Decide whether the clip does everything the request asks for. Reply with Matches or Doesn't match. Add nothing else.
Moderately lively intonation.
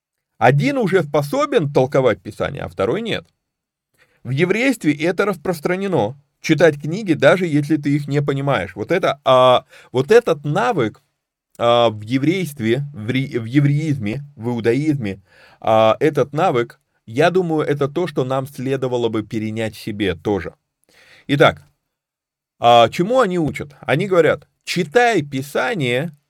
Doesn't match